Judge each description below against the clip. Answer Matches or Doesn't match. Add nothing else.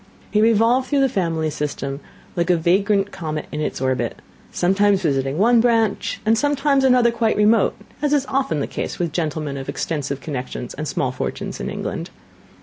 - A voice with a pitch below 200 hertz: Matches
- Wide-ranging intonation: Matches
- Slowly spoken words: Doesn't match